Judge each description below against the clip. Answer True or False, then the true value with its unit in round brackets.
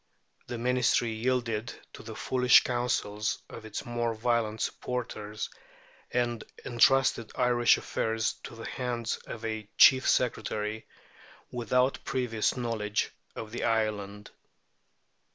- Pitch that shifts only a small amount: True (2.1 semitones)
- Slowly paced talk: True (115 wpm)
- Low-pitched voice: True (115 Hz)